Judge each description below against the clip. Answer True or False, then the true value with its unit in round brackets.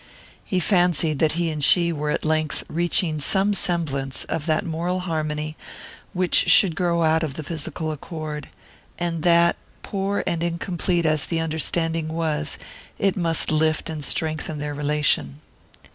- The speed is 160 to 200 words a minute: False (150 wpm)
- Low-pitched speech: False (160 Hz)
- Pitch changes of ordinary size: False (2.1 semitones)